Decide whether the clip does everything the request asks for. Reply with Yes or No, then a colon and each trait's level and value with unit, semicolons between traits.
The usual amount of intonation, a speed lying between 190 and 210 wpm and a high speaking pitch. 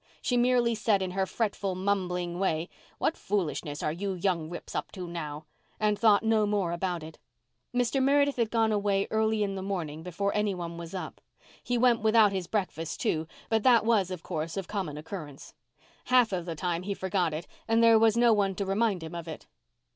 Yes: average, 4.2 semitones; fast, 205 wpm; high, 195 Hz